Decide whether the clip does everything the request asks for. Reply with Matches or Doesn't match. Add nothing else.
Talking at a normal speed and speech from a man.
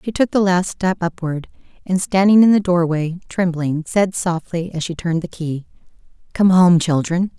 Doesn't match